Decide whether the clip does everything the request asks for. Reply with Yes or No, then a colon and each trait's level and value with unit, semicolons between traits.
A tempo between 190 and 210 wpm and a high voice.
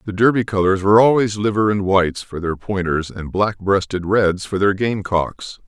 No: average, 200 wpm; low, 100 Hz